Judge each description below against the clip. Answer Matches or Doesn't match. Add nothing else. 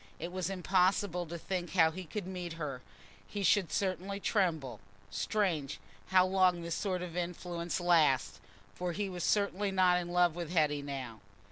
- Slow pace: Doesn't match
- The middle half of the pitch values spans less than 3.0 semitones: Matches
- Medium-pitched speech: Matches